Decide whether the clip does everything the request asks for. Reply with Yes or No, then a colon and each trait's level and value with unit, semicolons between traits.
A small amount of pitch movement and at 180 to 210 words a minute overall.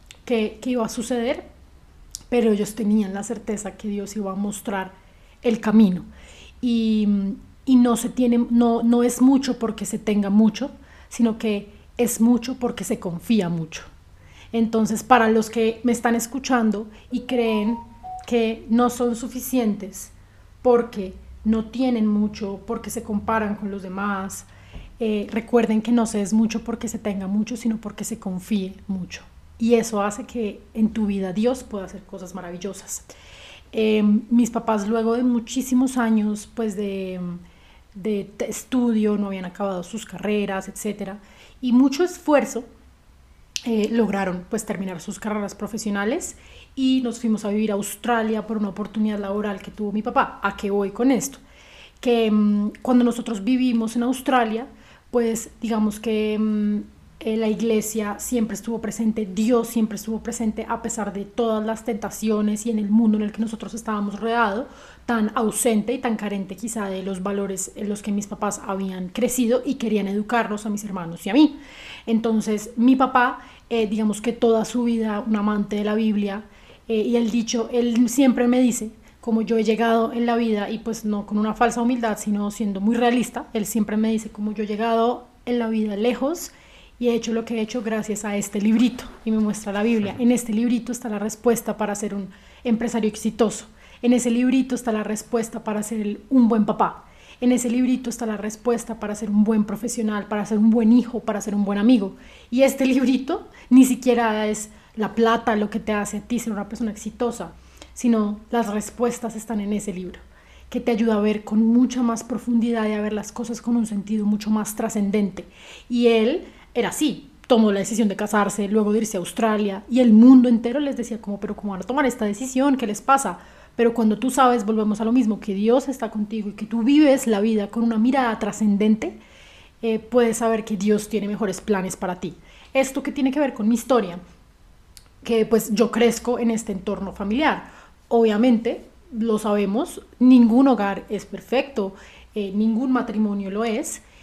Yes: narrow, 2.3 semitones; average, 185 wpm